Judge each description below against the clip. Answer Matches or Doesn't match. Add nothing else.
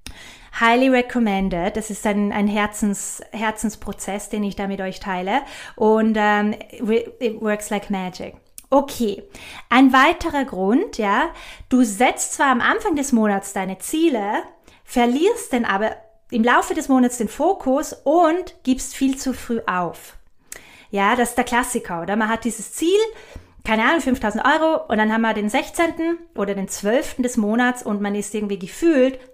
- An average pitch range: Matches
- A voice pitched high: Matches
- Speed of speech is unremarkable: Matches